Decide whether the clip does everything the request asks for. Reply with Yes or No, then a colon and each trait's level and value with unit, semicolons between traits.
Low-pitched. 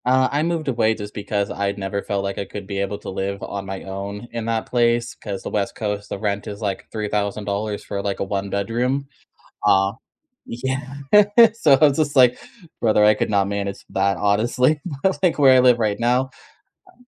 Yes: low, 105 Hz